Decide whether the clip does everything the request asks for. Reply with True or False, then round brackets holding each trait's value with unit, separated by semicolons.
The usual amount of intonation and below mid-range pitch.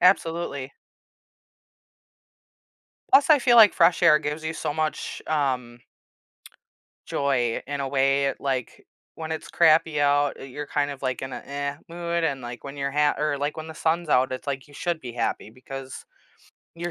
False (3.0 semitones; 145 Hz)